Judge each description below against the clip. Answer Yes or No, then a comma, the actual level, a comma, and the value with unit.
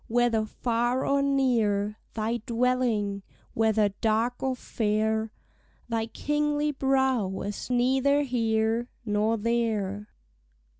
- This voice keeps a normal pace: No, slow, 100 wpm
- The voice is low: No, high, 230 Hz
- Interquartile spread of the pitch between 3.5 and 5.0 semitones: No, average, 2.9 semitones